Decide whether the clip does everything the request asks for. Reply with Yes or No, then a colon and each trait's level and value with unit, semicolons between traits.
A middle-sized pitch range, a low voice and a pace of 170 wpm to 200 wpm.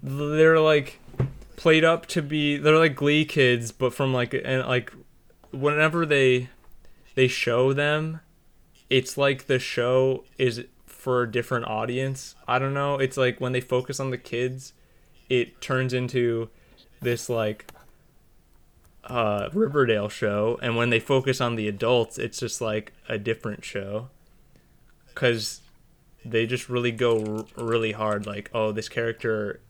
No: average, 3.1 semitones; low, 125 Hz; average, 150 wpm